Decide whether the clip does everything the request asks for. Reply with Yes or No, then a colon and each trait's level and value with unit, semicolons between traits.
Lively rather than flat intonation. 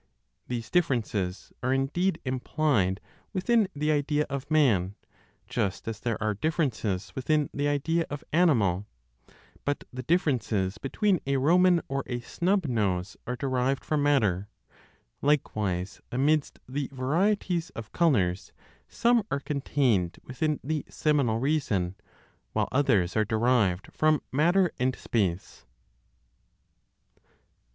Yes: wide, 6.0 semitones